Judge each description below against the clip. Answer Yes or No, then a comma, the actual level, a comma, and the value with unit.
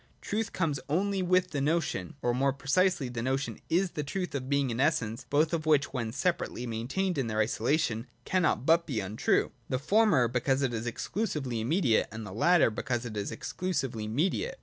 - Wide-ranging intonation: Yes, wide, 6.4 semitones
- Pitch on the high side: No, medium, 140 Hz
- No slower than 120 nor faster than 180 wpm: No, average, 190 wpm